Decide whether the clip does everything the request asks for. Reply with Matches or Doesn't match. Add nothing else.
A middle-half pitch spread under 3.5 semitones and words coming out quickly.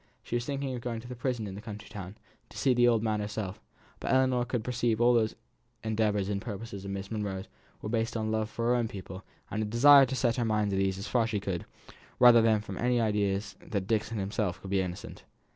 Matches